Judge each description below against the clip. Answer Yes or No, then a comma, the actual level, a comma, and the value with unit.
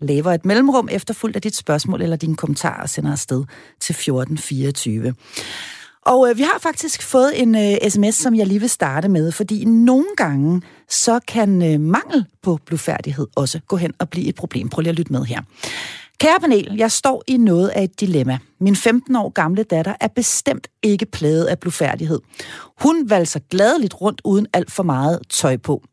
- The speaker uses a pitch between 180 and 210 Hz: Yes, medium, 185 Hz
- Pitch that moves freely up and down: Yes, wide, 6.4 semitones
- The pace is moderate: Yes, average, 190 wpm